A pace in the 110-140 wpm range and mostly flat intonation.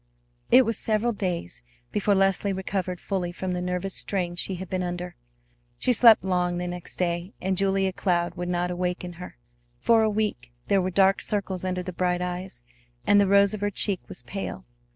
No: average, 195 wpm; narrow, 1.9 semitones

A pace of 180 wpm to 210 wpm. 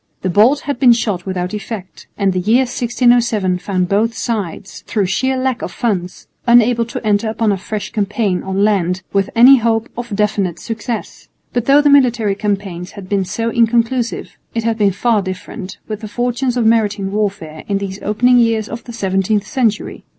Yes: average, 185 wpm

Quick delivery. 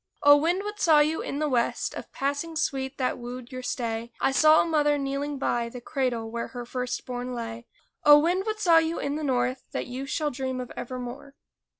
Yes: fast, 215 wpm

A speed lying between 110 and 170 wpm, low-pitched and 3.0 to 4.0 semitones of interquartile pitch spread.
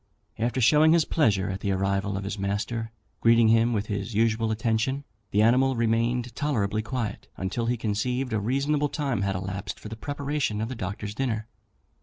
No: average, 180 wpm; low, 115 Hz; average, 3.7 semitones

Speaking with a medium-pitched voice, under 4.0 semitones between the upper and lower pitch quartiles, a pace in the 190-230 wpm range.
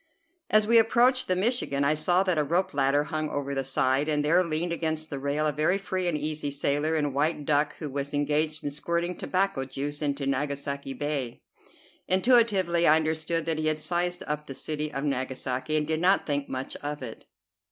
Yes: medium, 150 Hz; average, 3.2 semitones; average, 200 wpm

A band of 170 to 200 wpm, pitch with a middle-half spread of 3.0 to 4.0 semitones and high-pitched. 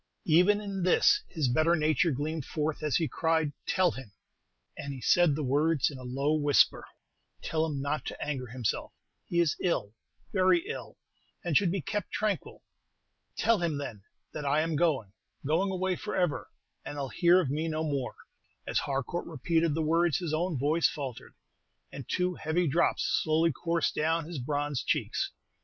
No: average, 175 wpm; average, 3.4 semitones; medium, 155 Hz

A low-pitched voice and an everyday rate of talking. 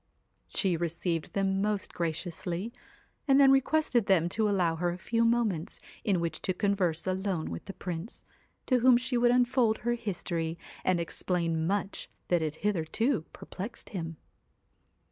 No: high, 190 Hz; average, 165 wpm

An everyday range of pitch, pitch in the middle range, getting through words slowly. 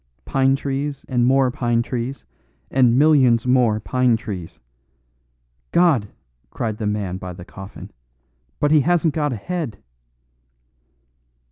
No: average, 4.7 semitones; low, 125 Hz; slow, 130 wpm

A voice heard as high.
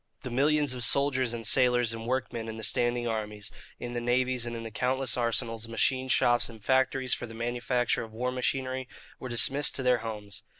No: low, 120 Hz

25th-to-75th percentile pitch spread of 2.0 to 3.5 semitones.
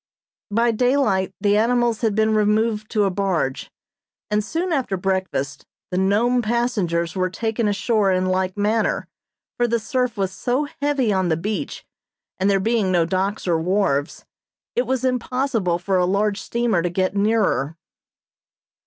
No: average, 3.9 semitones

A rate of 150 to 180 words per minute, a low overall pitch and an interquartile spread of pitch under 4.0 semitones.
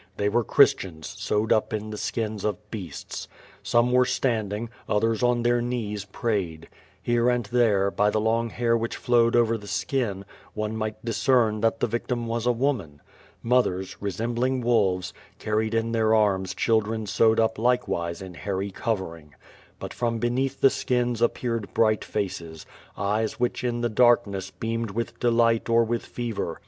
Yes: average, 155 wpm; low, 115 Hz; narrow, 2.6 semitones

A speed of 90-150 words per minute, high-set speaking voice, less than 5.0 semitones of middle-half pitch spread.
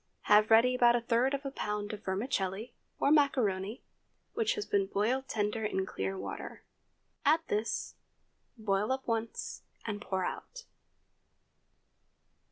Yes: slow, 135 wpm; high, 225 Hz; average, 4.2 semitones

